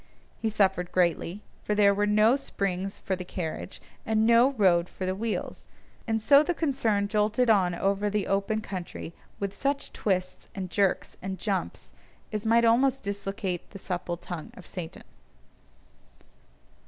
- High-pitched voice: Yes, high, 200 Hz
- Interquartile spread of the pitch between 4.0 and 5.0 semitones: No, average, 3.0 semitones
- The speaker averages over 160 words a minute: No, average, 155 wpm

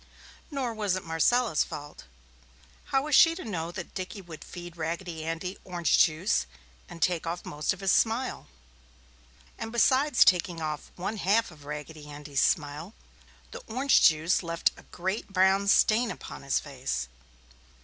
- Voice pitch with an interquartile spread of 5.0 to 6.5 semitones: Yes, average, 5.3 semitones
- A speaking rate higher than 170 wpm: No, average, 155 wpm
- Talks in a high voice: No, medium, 175 Hz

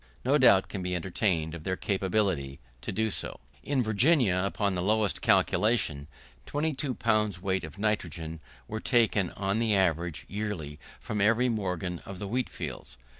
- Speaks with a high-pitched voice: No, low, 100 Hz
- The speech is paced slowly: No, average, 160 wpm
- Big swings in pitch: No, average, 3.7 semitones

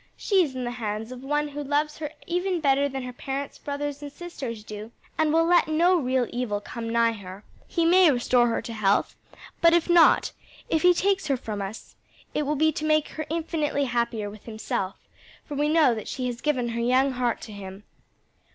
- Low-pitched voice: No, very high, 270 Hz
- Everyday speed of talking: No, fast, 210 wpm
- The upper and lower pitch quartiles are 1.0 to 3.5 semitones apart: No, average, 4.9 semitones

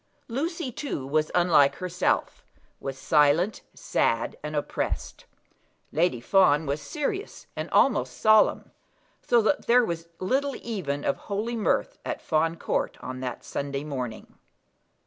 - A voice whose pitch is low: No, medium, 170 Hz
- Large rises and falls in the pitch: Yes, wide, 8.1 semitones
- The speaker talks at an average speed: No, slow, 130 wpm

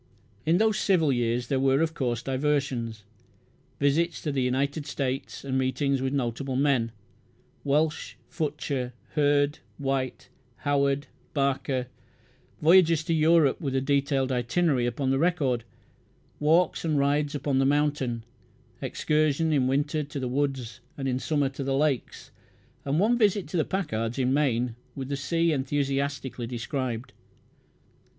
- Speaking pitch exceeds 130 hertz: Yes, medium, 140 Hz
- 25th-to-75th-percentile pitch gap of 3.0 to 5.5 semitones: No, narrow, 2.5 semitones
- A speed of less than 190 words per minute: Yes, average, 140 wpm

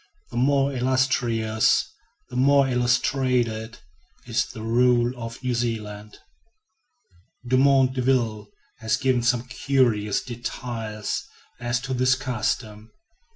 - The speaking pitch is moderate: No, low, 120 Hz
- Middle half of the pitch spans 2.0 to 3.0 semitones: Yes, narrow, 2.4 semitones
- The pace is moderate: No, slow, 105 wpm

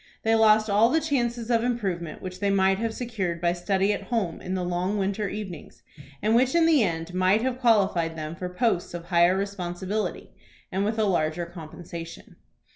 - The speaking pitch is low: No, high, 195 Hz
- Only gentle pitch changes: No, average, 4.2 semitones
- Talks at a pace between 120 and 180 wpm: No, average, 190 wpm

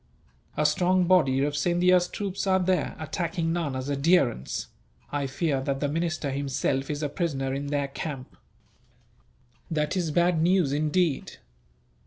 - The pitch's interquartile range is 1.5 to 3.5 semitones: No, average, 4.1 semitones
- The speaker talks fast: No, average, 140 wpm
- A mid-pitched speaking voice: Yes, medium, 150 Hz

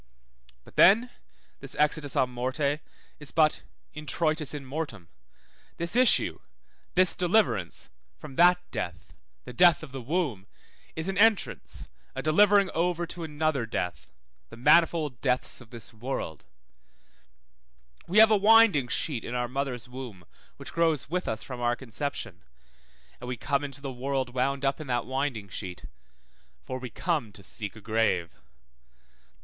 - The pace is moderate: Yes, average, 150 wpm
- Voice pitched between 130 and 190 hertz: Yes, medium, 140 Hz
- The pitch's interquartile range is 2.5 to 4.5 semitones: No, average, 5.2 semitones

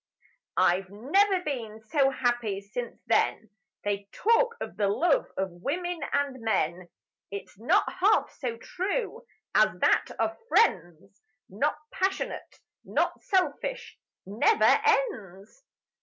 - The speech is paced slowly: Yes, slow, 115 wpm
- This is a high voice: Yes, very high, 250 Hz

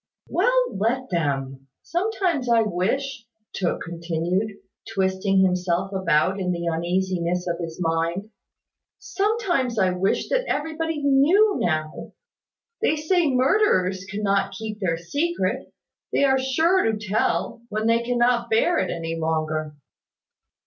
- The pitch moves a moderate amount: No, wide, 8.0 semitones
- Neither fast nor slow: No, slow, 125 wpm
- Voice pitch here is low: No, high, 205 Hz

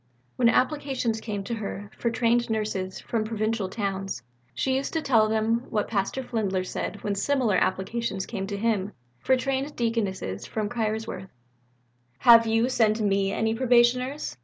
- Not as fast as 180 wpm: Yes, average, 155 wpm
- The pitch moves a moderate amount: Yes, average, 3.0 semitones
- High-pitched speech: Yes, high, 220 Hz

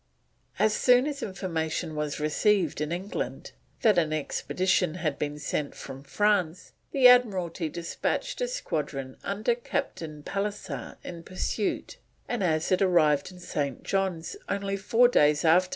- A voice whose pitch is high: No, medium, 180 Hz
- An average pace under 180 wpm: Yes, average, 145 wpm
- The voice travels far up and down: No, average, 5.0 semitones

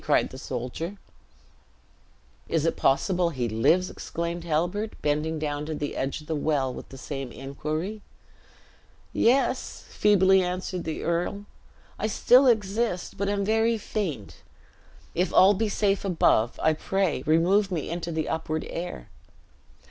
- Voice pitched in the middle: Yes, medium, 170 Hz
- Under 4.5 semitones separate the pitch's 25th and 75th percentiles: No, average, 4.8 semitones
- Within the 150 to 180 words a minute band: No, average, 140 wpm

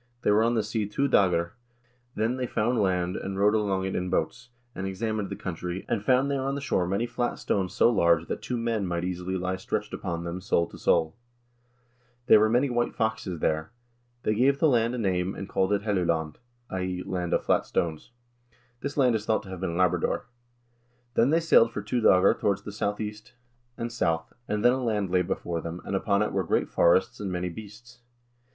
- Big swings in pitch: No, average, 4.2 semitones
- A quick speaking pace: Yes, fast, 210 wpm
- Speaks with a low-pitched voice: Yes, low, 100 Hz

